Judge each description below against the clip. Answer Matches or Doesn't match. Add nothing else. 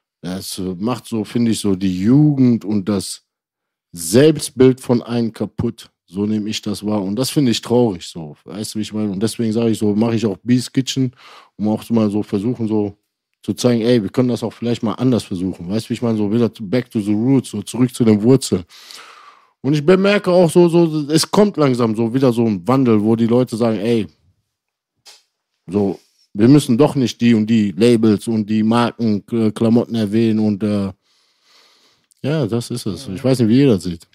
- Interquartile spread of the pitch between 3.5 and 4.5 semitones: Doesn't match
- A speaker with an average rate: Doesn't match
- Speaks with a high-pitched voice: Doesn't match